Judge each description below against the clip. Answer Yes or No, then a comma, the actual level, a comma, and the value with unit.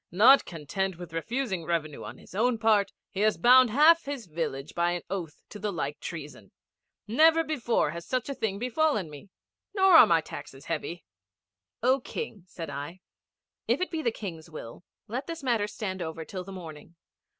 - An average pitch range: No, wide, 7.1 semitones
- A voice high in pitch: Yes, high, 195 Hz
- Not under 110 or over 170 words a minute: No, average, 185 wpm